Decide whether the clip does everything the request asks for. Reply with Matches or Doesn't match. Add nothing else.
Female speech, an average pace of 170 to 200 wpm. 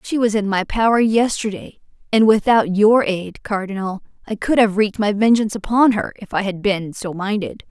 Matches